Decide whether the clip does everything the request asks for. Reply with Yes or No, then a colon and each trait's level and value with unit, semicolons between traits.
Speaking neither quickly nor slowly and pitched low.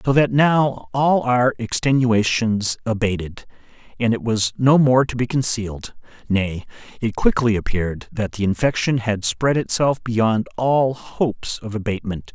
Yes: average, 145 wpm; low, 115 Hz